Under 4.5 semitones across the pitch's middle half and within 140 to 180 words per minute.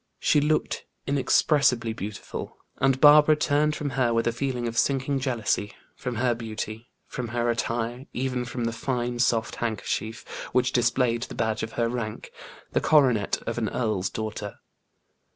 Yes: average, 2.7 semitones; average, 155 wpm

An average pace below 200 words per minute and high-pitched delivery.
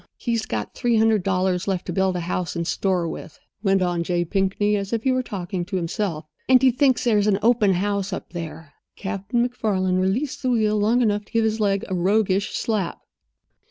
No: fast, 205 wpm; high, 195 Hz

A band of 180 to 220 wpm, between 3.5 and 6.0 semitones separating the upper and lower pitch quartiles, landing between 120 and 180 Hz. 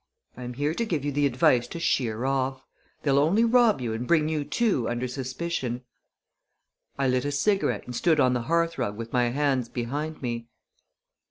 Yes: average, 185 wpm; average, 4.3 semitones; low, 135 Hz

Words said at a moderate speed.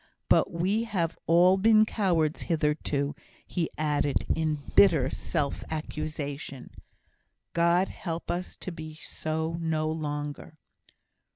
No: slow, 110 wpm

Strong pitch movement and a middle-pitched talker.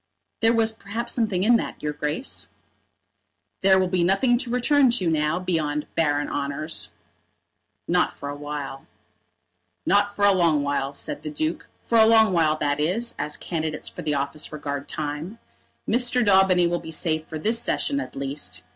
Yes: wide, 6.8 semitones; medium, 170 Hz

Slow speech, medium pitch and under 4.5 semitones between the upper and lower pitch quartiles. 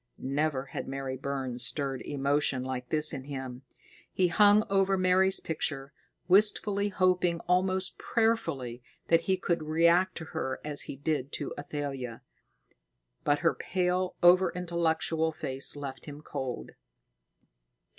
No: slow, 130 wpm; medium, 155 Hz; average, 5.0 semitones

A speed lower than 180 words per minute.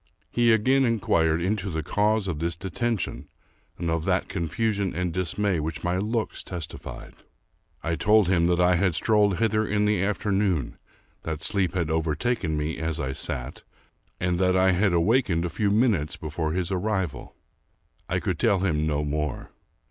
Yes: average, 170 wpm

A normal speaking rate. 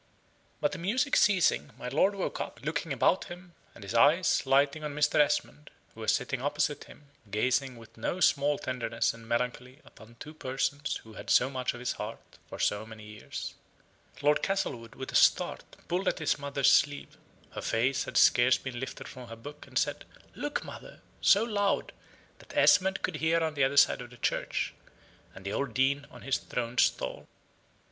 Yes: average, 190 wpm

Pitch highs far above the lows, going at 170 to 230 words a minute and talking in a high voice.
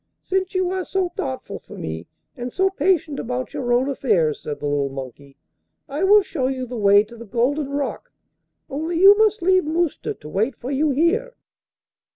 Yes: wide, 8.7 semitones; average, 190 wpm; very high, 275 Hz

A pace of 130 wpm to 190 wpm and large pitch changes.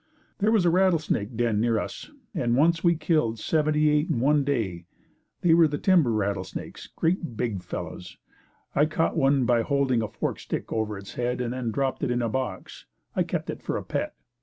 No: average, 200 wpm; wide, 5.7 semitones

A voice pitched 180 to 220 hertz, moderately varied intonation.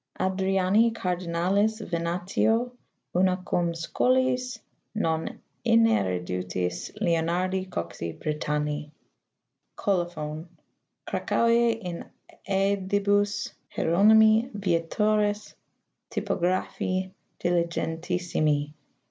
Yes: medium, 185 Hz; average, 3.9 semitones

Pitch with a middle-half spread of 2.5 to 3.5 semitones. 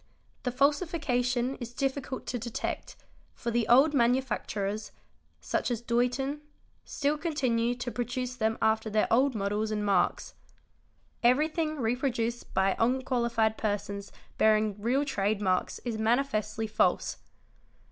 Yes: average, 3.2 semitones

